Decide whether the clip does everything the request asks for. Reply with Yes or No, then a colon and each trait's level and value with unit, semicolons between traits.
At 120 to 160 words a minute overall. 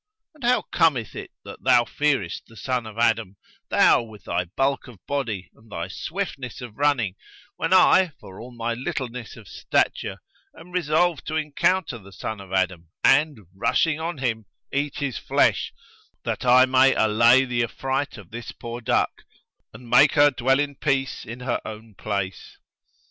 No: average, 170 wpm